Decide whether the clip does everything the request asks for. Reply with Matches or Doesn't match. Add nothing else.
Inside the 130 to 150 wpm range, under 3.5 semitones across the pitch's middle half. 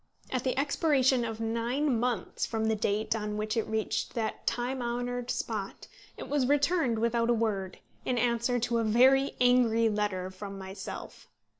Doesn't match